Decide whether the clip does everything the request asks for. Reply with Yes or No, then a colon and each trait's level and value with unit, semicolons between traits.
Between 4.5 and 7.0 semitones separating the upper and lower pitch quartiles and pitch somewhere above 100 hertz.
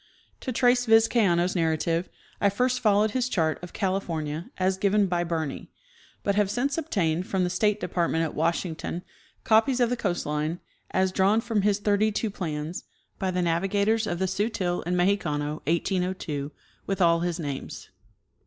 No: average, 3.8 semitones; medium, 185 Hz